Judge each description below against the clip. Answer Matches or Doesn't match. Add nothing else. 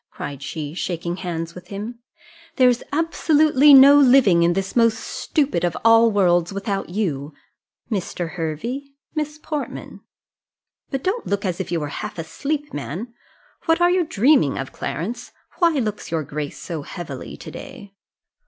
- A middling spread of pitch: Doesn't match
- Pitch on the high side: Matches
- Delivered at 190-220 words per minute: Doesn't match